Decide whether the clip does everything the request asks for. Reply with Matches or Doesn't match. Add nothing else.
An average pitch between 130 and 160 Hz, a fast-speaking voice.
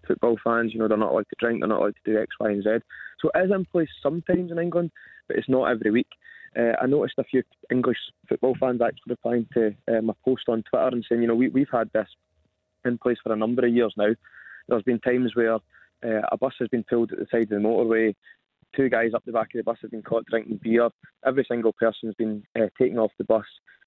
Doesn't match